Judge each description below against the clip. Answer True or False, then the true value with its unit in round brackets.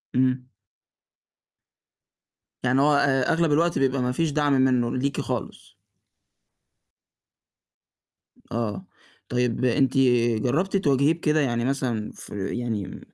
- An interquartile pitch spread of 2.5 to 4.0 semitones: True (3.0 semitones)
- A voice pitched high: False (130 Hz)